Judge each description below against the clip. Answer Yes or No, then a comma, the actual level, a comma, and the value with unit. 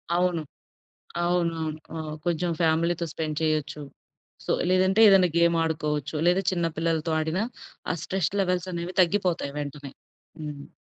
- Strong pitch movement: No, narrow, 2.5 semitones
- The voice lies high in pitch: No, medium, 170 Hz